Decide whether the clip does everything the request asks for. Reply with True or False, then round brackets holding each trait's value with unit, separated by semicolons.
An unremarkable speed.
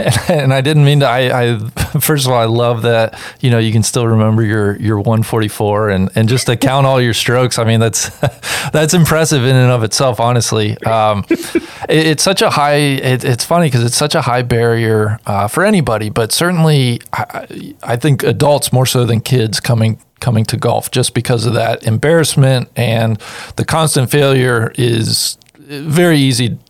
True (195 wpm)